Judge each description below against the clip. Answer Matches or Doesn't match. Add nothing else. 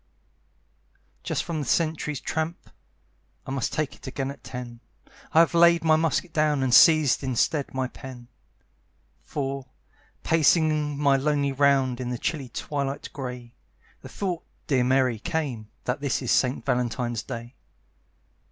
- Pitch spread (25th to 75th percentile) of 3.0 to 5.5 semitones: Matches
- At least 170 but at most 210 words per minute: Doesn't match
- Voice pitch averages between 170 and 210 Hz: Doesn't match